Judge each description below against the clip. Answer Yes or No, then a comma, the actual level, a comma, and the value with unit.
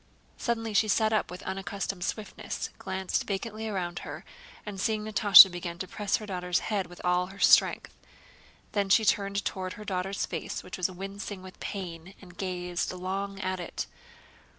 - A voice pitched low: No, high, 195 Hz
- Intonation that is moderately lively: No, narrow, 2.1 semitones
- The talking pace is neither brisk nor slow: Yes, average, 170 wpm